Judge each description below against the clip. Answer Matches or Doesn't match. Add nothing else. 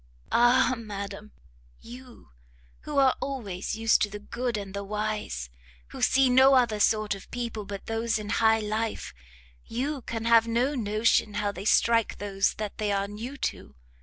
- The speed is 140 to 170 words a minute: Matches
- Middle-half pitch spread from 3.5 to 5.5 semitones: Doesn't match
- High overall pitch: Matches